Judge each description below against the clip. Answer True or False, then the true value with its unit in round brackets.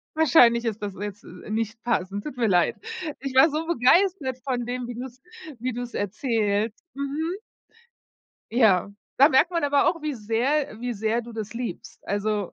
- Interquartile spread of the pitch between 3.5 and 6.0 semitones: True (4.2 semitones)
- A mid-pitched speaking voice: False (240 Hz)